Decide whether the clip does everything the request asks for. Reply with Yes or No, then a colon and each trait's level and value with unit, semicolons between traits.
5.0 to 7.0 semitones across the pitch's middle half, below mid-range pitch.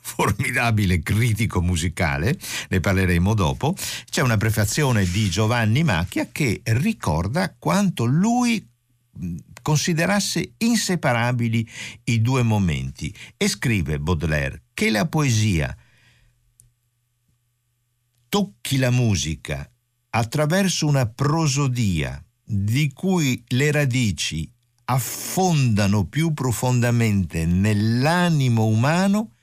Yes: wide, 5.5 semitones; low, 120 Hz